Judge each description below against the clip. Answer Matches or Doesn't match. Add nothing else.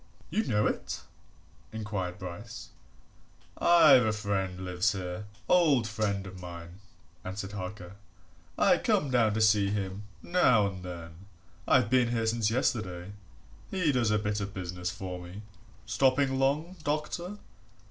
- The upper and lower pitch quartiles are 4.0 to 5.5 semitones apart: Matches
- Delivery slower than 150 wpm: Matches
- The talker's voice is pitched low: Matches